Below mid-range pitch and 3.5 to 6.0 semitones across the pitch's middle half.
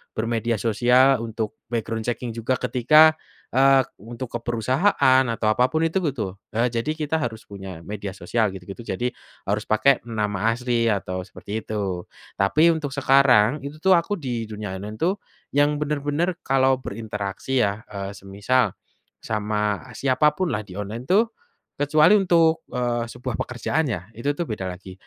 Yes: low, 120 Hz; average, 4.8 semitones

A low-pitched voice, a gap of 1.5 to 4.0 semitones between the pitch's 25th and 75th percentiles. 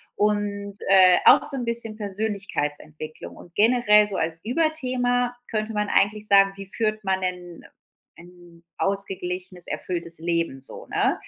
No: high, 200 Hz; average, 3.4 semitones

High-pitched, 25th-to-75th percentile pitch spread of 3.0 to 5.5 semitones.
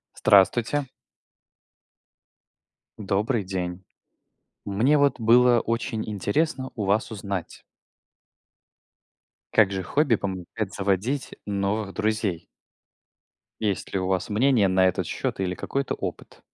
No: low, 105 Hz; average, 3.8 semitones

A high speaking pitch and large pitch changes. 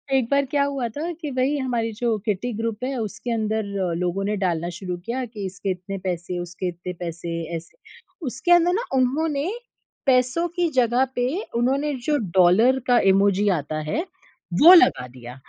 Yes: high, 230 Hz; wide, 6.8 semitones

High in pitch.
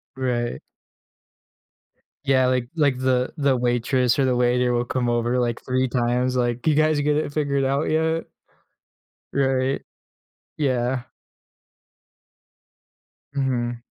No: low, 130 Hz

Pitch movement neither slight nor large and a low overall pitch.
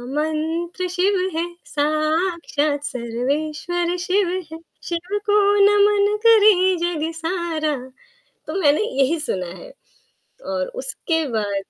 No: average, 3.5 semitones; very high, 335 Hz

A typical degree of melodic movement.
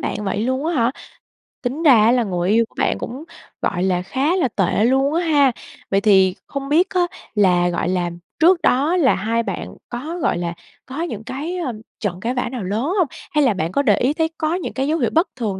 No: wide, 7.3 semitones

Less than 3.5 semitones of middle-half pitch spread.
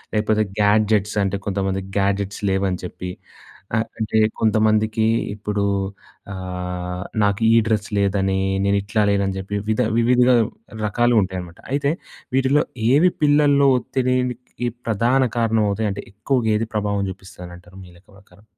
Yes: average, 2.8 semitones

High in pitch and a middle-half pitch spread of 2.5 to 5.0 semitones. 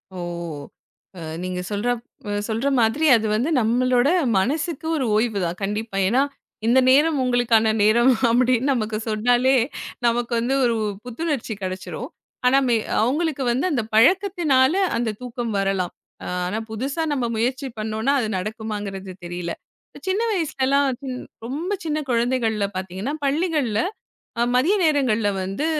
Yes: high, 240 Hz; average, 4.1 semitones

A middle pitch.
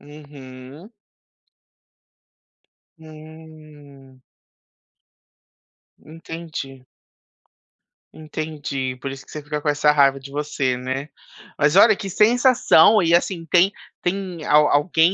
Yes: medium, 150 Hz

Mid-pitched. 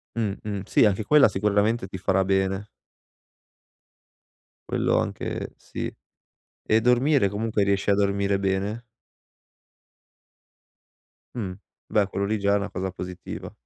No: low, 100 Hz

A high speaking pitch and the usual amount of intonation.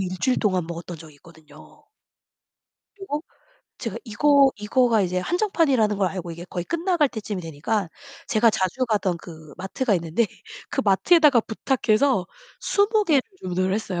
No: high, 210 Hz; wide, 7.0 semitones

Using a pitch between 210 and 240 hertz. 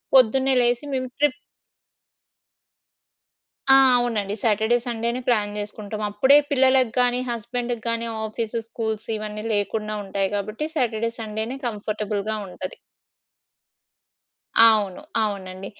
Yes: high, 220 Hz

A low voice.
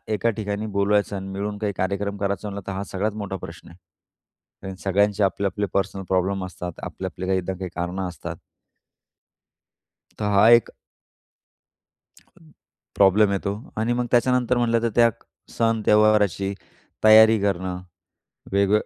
Yes: low, 100 Hz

